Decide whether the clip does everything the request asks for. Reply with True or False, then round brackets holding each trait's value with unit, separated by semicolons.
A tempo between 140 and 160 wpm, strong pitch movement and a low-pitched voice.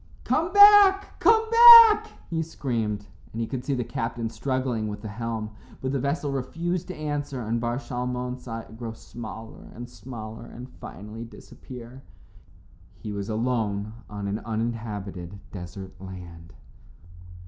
False (145 wpm; 4.3 semitones; 120 Hz)